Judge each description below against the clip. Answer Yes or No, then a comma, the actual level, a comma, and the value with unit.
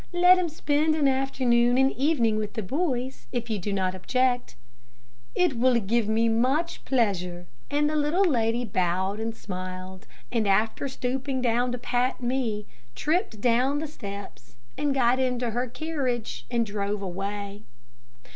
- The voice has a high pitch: Yes, high, 240 Hz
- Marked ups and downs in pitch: No, average, 4.5 semitones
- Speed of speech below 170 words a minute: Yes, average, 155 wpm